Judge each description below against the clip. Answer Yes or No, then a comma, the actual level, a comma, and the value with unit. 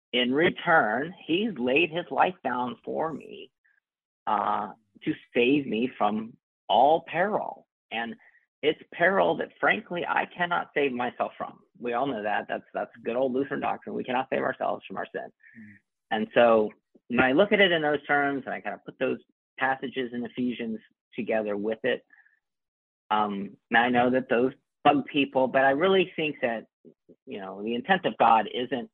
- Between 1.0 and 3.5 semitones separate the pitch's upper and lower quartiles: No, average, 4.2 semitones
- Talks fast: No, average, 175 wpm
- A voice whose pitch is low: Yes, low, 130 Hz